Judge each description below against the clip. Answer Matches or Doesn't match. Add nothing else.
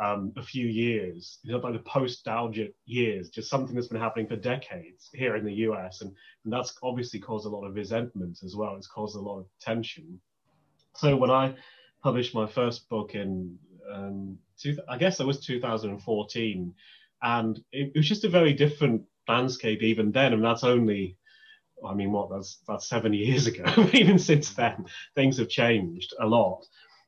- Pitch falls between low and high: Doesn't match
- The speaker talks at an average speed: Matches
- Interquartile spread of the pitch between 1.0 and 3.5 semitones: Doesn't match